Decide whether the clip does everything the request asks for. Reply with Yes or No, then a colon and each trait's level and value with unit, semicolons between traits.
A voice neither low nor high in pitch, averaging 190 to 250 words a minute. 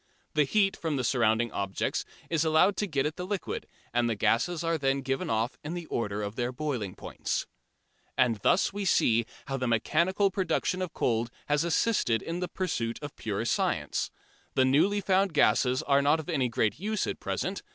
Yes: medium, 145 Hz; average, 195 wpm